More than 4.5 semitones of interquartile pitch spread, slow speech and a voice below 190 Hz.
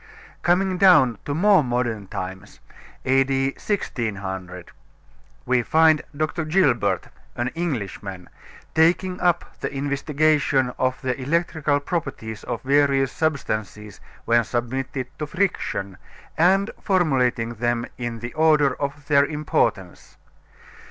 Yes: average, 4.9 semitones; slow, 110 wpm; low, 135 Hz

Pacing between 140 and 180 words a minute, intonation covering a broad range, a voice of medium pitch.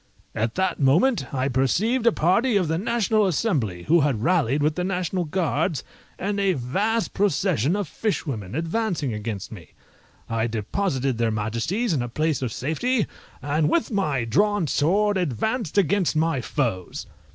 Yes: average, 155 wpm; wide, 7.7 semitones; medium, 160 Hz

